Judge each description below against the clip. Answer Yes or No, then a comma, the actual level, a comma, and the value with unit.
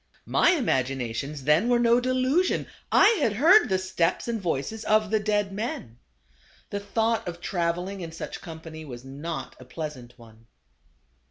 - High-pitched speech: No, medium, 180 Hz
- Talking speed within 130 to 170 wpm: Yes, average, 160 wpm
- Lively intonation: Yes, wide, 7.7 semitones